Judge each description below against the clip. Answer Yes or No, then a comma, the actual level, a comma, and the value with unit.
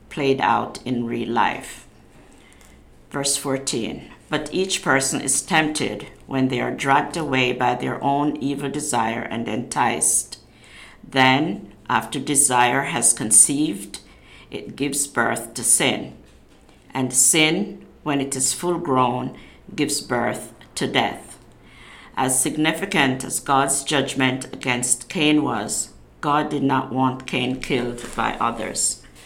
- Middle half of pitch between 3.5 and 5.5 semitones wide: No, average, 2.7 semitones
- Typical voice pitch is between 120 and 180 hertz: Yes, low, 135 Hz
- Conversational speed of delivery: No, slow, 125 wpm